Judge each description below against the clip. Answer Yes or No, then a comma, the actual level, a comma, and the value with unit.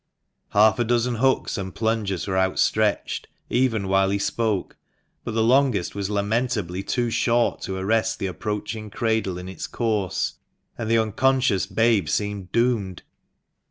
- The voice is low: Yes, low, 110 Hz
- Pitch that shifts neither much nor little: Yes, average, 3.1 semitones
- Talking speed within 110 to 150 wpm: Yes, average, 145 wpm